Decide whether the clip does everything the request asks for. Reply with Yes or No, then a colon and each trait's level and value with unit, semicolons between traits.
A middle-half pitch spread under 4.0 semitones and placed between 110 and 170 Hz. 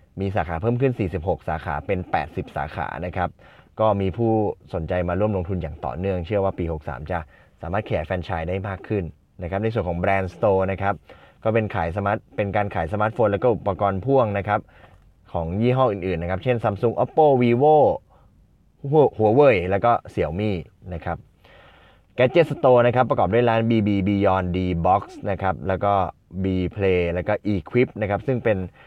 No: average, 3.6 semitones; low, 100 Hz